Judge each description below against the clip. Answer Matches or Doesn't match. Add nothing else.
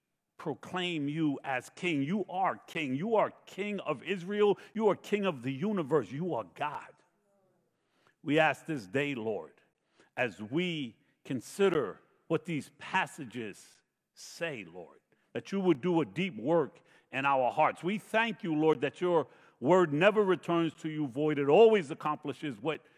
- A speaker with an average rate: Matches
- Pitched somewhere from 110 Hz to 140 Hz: Doesn't match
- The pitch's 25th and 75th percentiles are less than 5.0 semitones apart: Matches